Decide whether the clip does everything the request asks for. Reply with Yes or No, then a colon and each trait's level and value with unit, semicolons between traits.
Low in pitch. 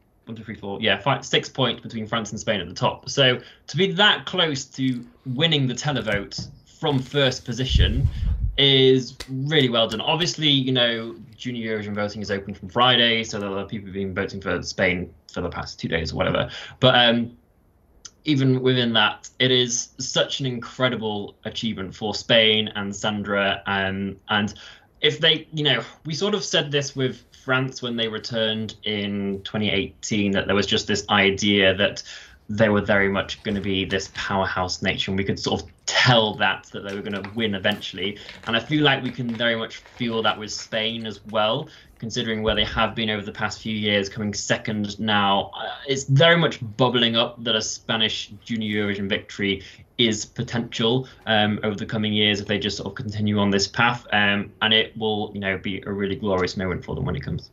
Yes: low, 110 Hz